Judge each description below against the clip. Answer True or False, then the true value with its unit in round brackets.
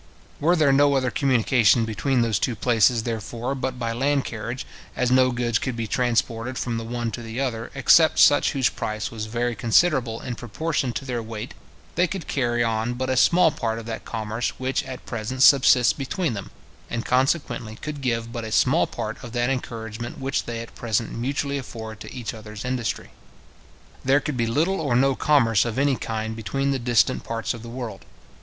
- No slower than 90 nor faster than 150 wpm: False (195 wpm)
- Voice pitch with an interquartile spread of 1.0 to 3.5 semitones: True (2.8 semitones)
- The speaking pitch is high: False (120 Hz)